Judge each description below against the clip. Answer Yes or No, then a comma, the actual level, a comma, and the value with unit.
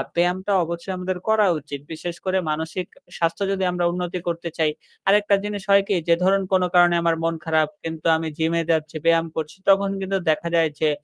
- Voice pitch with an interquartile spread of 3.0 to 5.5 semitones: No, narrow, 2.6 semitones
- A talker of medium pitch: Yes, medium, 170 Hz